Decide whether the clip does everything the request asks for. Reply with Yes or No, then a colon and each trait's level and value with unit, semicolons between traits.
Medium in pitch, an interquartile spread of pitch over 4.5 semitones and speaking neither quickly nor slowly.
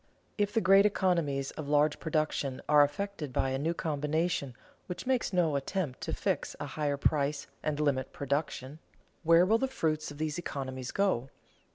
No: medium, 150 Hz; average, 3.9 semitones; average, 175 wpm